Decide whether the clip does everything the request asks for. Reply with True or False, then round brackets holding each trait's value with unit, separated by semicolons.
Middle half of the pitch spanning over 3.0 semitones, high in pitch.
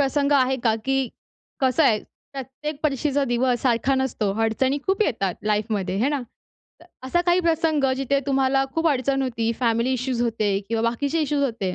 True (3.4 semitones; 265 Hz)